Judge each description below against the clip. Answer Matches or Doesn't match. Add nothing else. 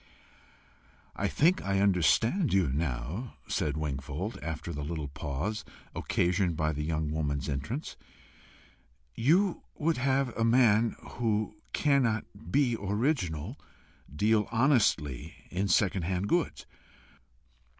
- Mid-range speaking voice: Doesn't match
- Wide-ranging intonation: Matches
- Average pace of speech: Doesn't match